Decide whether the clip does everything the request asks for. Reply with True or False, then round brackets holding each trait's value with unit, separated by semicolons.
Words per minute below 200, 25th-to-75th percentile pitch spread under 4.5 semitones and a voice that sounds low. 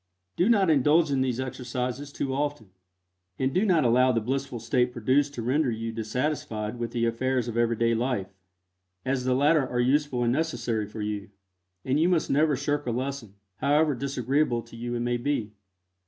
True (185 wpm; 3.5 semitones; 130 Hz)